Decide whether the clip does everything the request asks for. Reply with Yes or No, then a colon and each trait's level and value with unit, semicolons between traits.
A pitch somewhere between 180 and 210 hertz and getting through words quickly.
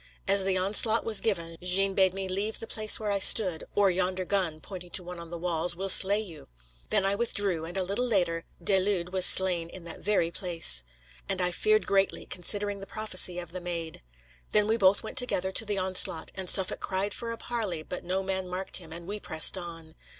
Yes: high, 190 Hz; fast, 220 wpm